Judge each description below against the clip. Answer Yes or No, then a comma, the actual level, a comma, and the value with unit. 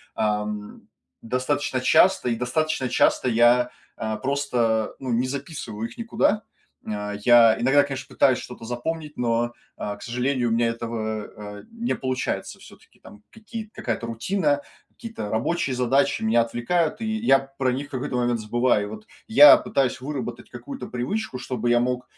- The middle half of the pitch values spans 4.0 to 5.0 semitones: No, average, 3.6 semitones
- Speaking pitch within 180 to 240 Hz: No, low, 125 Hz